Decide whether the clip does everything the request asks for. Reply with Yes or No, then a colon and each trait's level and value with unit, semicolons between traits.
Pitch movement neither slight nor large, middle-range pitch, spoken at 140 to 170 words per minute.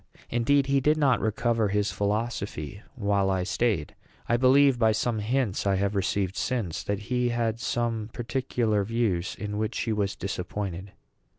No: average, 3.1 semitones; low, 110 Hz; average, 160 wpm